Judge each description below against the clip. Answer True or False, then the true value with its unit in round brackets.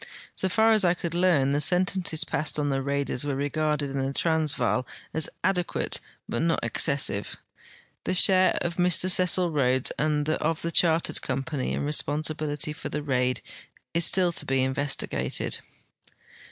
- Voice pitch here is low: False (155 Hz)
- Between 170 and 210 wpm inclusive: False (160 wpm)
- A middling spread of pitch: True (3.6 semitones)